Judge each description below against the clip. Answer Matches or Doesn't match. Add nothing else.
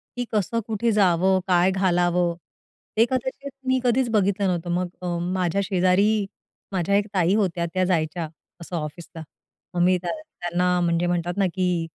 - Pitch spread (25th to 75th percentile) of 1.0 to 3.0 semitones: Matches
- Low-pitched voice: Doesn't match